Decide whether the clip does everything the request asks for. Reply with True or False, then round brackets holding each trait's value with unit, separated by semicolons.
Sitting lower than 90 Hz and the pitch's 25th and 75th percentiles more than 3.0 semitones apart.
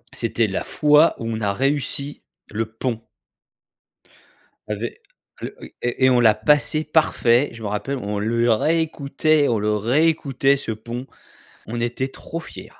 False (120 Hz; 4.4 semitones)